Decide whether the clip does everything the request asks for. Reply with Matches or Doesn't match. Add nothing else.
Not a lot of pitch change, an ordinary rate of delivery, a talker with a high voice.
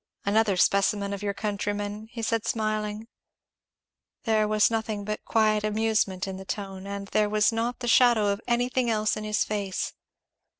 Matches